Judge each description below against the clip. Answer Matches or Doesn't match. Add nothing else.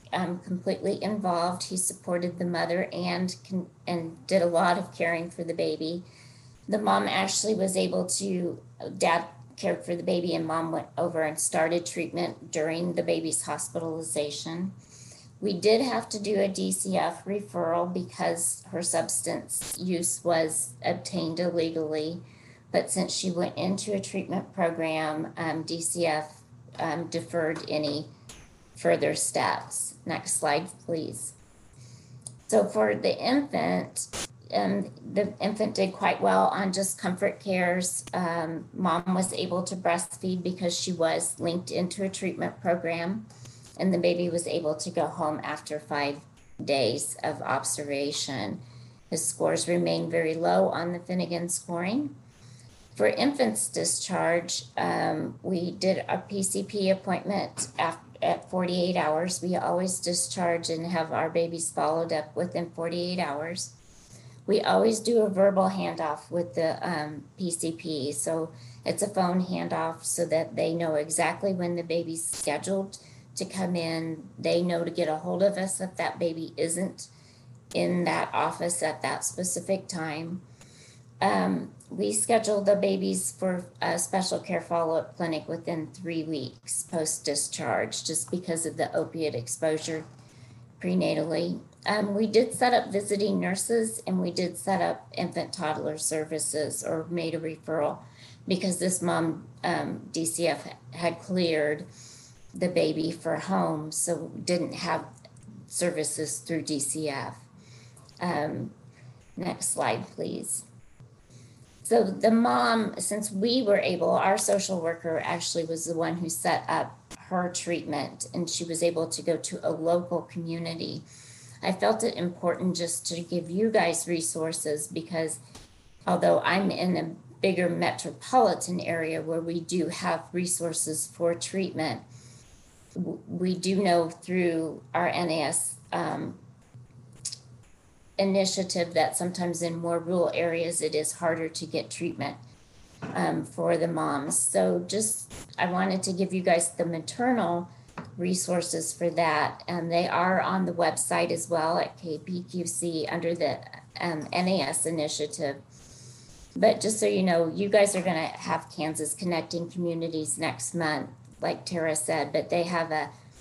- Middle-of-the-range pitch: Matches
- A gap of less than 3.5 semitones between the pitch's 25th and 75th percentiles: Matches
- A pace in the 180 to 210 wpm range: Doesn't match